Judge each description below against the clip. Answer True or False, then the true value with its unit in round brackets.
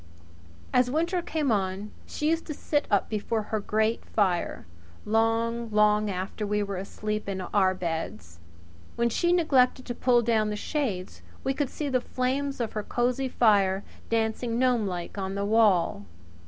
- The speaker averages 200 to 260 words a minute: False (160 wpm)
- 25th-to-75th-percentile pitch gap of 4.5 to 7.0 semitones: False (4.0 semitones)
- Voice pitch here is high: True (220 Hz)